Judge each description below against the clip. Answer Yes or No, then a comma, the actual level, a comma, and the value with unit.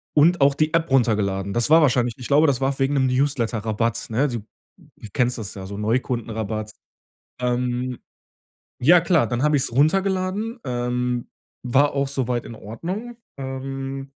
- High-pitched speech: No, low, 130 Hz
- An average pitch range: Yes, average, 3.7 semitones